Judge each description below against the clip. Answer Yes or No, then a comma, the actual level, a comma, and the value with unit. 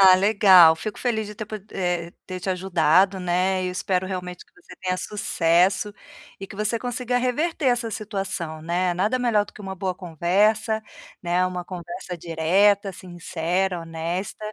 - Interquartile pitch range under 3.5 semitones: Yes, average, 3.0 semitones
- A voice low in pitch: No, medium, 185 Hz